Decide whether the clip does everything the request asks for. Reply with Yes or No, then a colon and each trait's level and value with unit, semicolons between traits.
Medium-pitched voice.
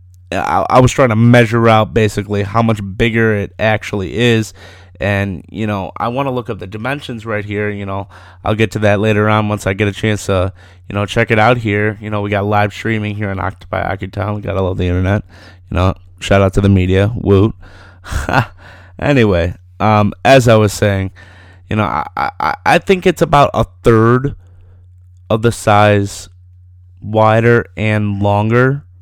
No: low, 105 Hz